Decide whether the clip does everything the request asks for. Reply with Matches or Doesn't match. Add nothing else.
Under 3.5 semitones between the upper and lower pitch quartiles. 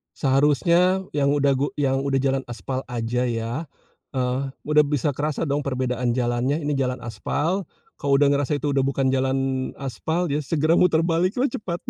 Matches